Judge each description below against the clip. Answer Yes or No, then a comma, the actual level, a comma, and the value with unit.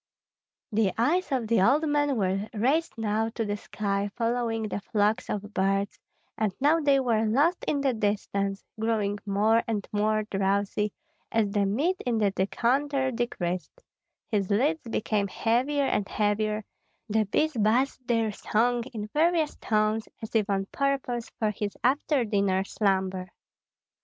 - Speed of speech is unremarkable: Yes, average, 150 wpm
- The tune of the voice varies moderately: Yes, average, 4.0 semitones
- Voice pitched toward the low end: No, high, 220 Hz